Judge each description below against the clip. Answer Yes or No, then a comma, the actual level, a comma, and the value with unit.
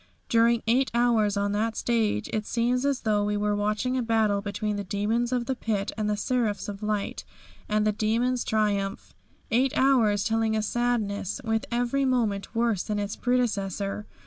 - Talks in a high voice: Yes, high, 220 Hz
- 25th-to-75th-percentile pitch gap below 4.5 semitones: Yes, narrow, 2.6 semitones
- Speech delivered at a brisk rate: No, average, 175 wpm